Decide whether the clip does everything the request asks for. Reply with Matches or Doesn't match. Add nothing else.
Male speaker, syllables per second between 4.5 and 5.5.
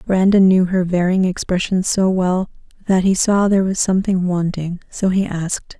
Doesn't match